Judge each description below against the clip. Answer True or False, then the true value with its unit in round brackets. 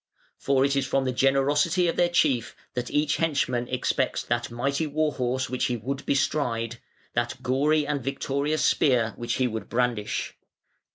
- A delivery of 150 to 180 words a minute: True (165 wpm)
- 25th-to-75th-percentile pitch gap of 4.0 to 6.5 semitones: False (3.1 semitones)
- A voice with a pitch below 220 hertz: True (135 Hz)